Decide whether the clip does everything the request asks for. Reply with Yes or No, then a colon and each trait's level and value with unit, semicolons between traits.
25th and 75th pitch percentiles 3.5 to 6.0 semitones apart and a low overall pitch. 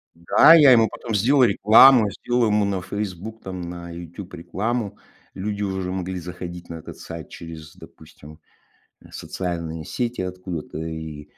Yes: average, 3.9 semitones; very low, 95 Hz